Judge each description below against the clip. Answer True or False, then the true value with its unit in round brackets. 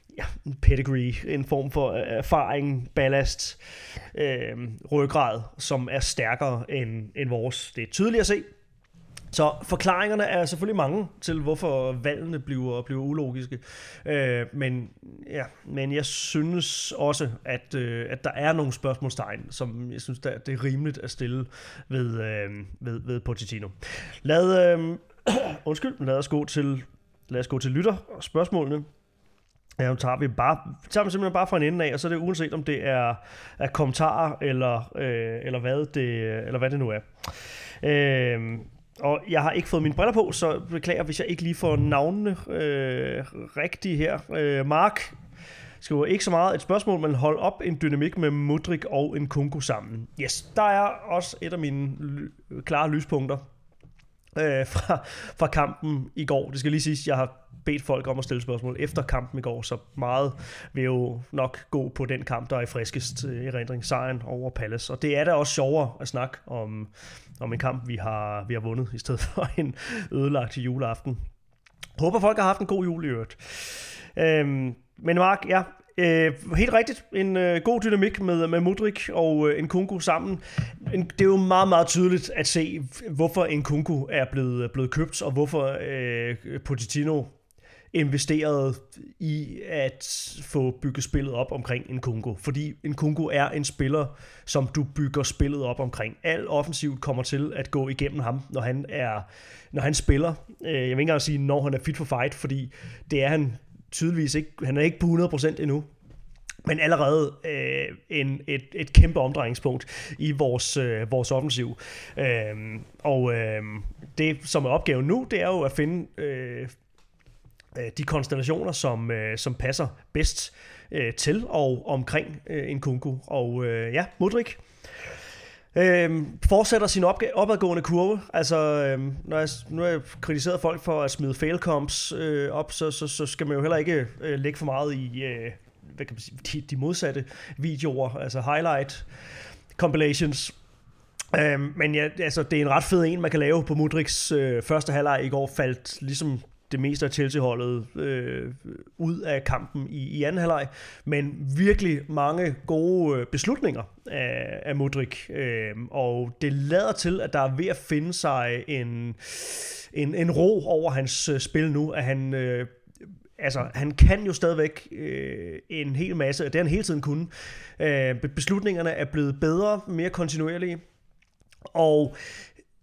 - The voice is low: False (145 Hz)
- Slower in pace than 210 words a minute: True (170 wpm)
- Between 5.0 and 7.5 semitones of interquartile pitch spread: False (3.6 semitones)